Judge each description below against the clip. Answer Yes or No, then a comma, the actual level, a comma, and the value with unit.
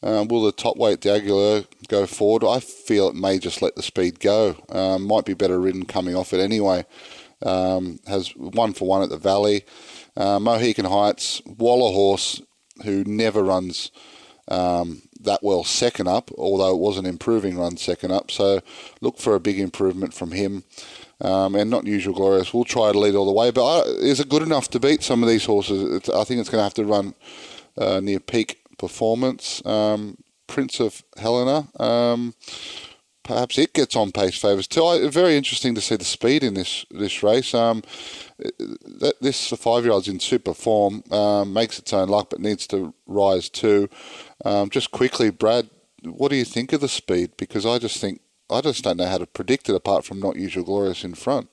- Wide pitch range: No, average, 3.3 semitones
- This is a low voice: Yes, low, 105 Hz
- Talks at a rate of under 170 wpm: No, average, 200 wpm